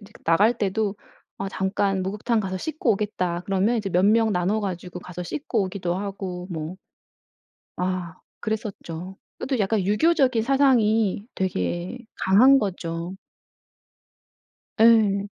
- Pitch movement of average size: Yes, average, 3.3 semitones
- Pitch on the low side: No, high, 195 Hz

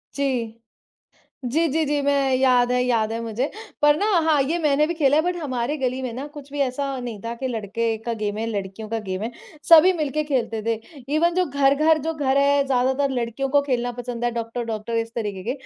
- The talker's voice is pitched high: Yes, very high, 260 Hz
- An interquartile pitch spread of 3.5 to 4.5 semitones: Yes, average, 3.8 semitones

